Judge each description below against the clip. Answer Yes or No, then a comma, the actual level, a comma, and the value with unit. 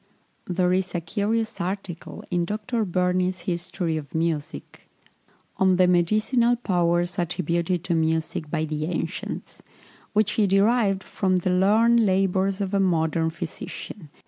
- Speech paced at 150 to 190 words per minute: No, average, 140 wpm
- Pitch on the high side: No, medium, 180 Hz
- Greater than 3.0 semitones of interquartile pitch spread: No, average, 2.7 semitones